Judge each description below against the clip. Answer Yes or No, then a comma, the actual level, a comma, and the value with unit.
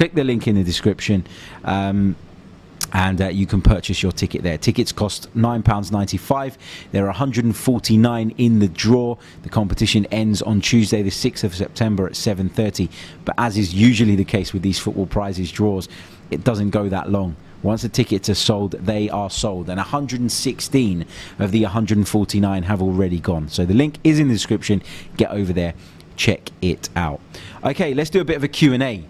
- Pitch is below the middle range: Yes, low, 105 Hz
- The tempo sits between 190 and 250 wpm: No, average, 180 wpm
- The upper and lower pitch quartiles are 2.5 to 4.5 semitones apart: Yes, average, 3.5 semitones